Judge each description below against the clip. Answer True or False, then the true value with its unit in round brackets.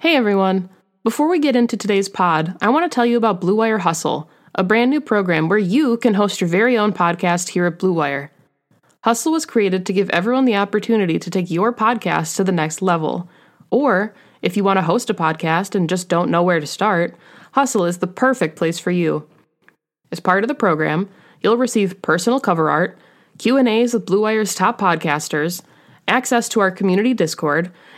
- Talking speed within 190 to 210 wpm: True (195 wpm)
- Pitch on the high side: True (195 Hz)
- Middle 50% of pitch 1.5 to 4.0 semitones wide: False (4.7 semitones)